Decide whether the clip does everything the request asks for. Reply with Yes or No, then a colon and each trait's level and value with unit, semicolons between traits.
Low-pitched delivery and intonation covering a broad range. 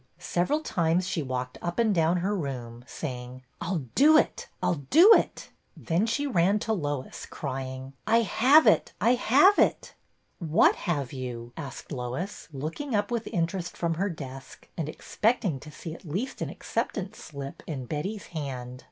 No: medium, 165 Hz; wide, 7.5 semitones